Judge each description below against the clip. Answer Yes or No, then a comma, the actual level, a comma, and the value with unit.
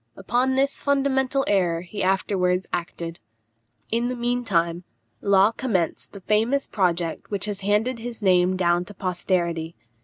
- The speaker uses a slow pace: No, average, 145 wpm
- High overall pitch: Yes, high, 195 Hz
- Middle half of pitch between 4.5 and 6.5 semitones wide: Yes, average, 5.1 semitones